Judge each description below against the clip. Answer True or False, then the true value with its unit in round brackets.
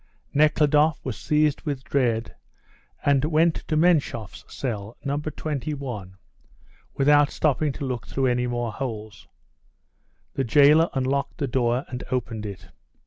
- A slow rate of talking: True (130 wpm)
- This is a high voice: False (135 Hz)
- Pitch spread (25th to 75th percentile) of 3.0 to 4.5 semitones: True (3.8 semitones)